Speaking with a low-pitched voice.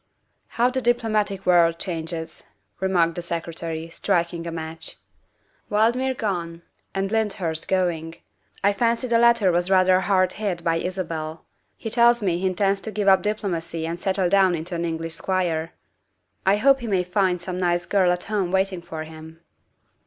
No: medium, 185 Hz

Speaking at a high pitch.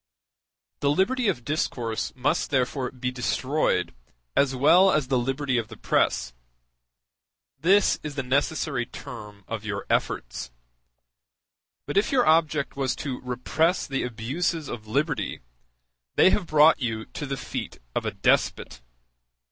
No: low, 135 Hz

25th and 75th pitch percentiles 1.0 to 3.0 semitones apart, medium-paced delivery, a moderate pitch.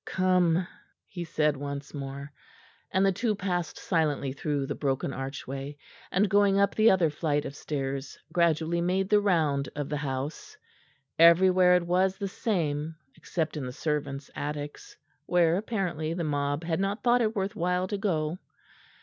No: average, 4.5 semitones; average, 160 wpm; medium, 165 Hz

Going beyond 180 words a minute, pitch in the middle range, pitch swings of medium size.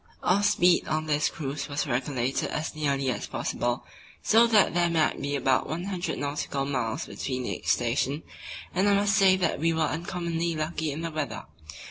No: average, 170 wpm; medium, 155 Hz; average, 4.0 semitones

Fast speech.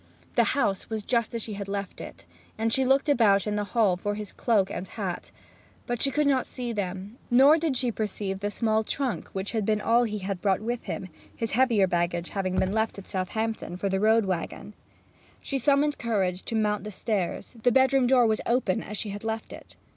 Yes: fast, 215 wpm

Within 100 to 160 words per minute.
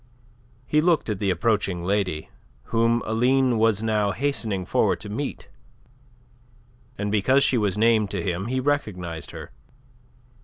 Yes: average, 140 wpm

